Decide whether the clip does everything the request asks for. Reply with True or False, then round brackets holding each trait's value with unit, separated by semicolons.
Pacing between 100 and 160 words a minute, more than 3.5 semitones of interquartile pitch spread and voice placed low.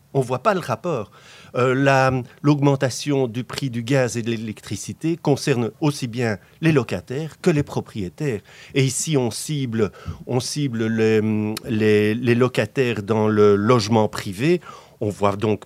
True (155 wpm; 4.2 semitones; 125 Hz)